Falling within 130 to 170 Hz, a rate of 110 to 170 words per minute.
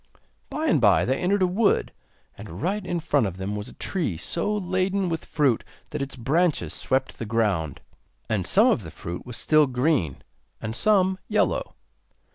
No: medium, 140 Hz; average, 180 wpm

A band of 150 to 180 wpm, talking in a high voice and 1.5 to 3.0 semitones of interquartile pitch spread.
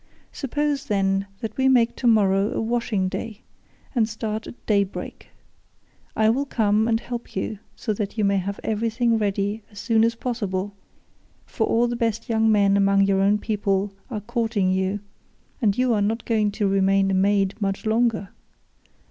Yes: average, 170 wpm; high, 215 Hz; average, 2.7 semitones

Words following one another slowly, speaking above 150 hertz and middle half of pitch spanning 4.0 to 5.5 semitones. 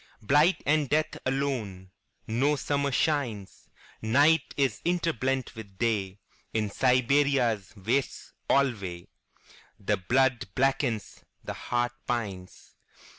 No: slow, 80 wpm; low, 125 Hz; average, 4.8 semitones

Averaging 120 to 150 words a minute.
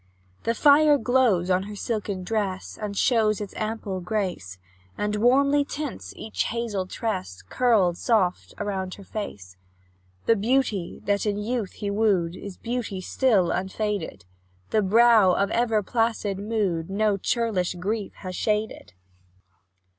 Yes: slow, 135 wpm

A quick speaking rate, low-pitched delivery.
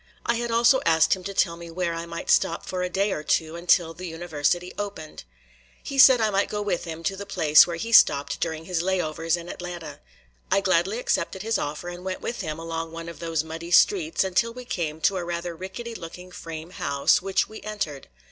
No: fast, 225 wpm; medium, 175 Hz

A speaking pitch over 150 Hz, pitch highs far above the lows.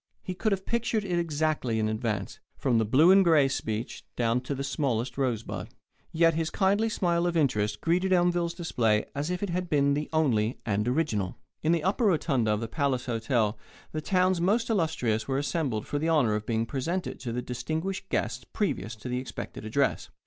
No: medium, 145 Hz; wide, 6.8 semitones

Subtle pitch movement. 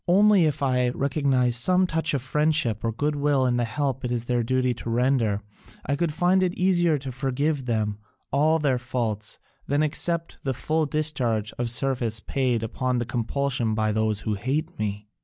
No: average, 4.4 semitones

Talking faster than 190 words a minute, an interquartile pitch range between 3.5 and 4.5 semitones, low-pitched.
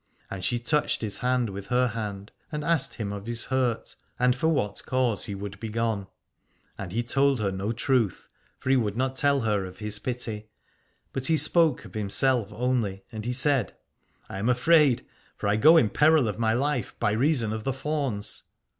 Yes: average, 200 wpm; average, 4.2 semitones; low, 120 Hz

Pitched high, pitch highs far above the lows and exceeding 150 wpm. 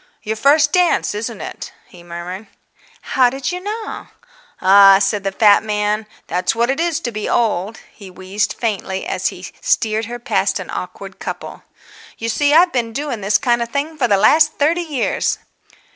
Yes: high, 230 Hz; wide, 6.1 semitones; average, 180 wpm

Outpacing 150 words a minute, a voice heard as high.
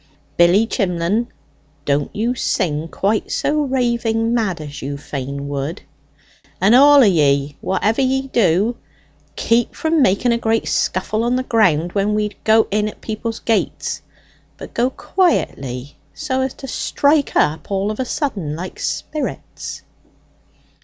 No: average, 145 wpm; high, 215 Hz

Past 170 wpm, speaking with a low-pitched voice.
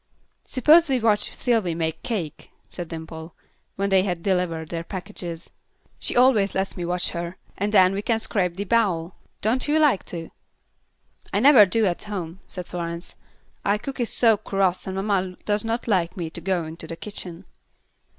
No: average, 180 wpm; high, 190 Hz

